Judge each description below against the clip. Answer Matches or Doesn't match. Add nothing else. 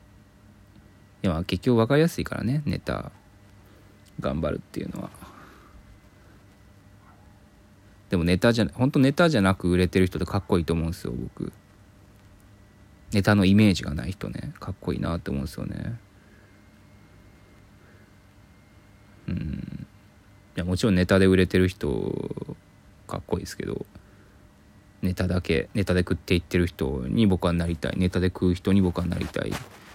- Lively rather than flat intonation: Doesn't match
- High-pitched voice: Doesn't match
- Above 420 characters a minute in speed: Doesn't match